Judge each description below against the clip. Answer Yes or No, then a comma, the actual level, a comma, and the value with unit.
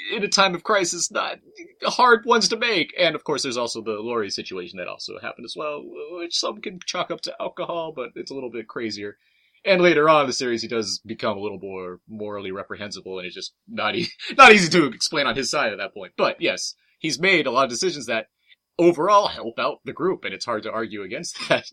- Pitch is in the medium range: Yes, medium, 170 Hz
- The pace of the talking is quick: Yes, fast, 240 wpm